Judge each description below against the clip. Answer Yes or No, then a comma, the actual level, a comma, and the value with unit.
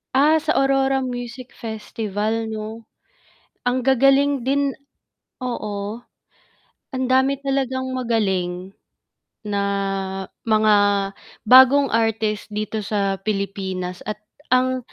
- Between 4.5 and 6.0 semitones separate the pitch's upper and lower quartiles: No, average, 3.9 semitones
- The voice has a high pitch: Yes, high, 230 Hz